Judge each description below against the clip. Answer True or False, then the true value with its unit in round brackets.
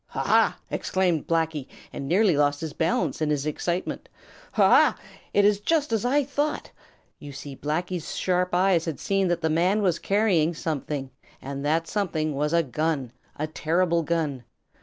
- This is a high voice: False (165 Hz)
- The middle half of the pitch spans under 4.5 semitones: True (3.7 semitones)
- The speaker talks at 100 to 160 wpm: False (170 wpm)